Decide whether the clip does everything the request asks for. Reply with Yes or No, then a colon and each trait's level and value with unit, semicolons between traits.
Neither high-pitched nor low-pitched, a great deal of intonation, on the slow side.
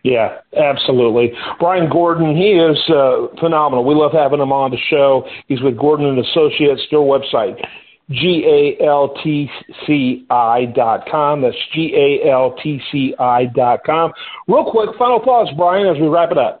No: medium, 150 Hz; average, 4.1 semitones; slow, 125 wpm